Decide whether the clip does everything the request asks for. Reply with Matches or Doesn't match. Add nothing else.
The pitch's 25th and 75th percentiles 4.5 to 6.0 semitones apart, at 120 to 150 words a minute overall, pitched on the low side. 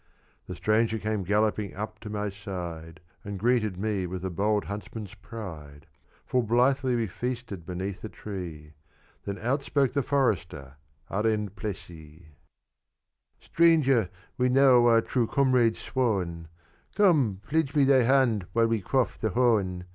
Matches